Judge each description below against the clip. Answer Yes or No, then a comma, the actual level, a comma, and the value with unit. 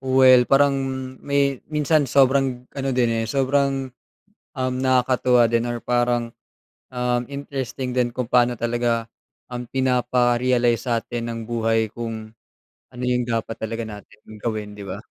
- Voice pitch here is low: Yes, low, 125 Hz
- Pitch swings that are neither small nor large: No, narrow, 2.0 semitones